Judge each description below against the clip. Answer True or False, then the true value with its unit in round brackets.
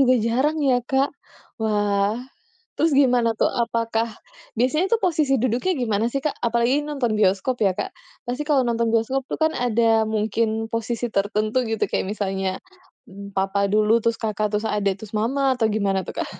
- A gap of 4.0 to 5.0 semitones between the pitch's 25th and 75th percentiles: False (3.3 semitones)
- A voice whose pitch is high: True (230 Hz)